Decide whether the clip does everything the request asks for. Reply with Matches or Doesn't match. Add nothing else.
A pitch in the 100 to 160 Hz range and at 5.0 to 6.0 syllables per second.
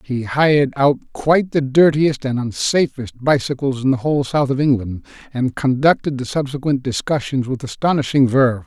Matches